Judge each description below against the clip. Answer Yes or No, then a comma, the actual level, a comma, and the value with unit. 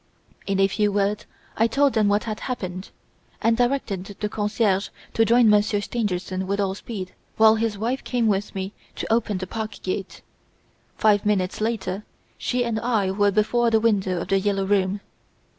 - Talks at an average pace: Yes, average, 175 wpm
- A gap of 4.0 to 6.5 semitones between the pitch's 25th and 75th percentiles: No, narrow, 2.6 semitones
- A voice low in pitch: No, high, 210 Hz